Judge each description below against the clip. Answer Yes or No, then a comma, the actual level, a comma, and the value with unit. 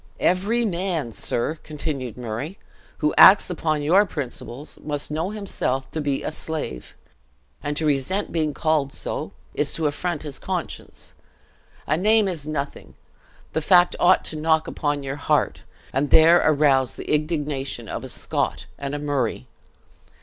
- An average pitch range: Yes, average, 3.3 semitones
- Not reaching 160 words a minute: Yes, average, 150 wpm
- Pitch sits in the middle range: Yes, medium, 150 Hz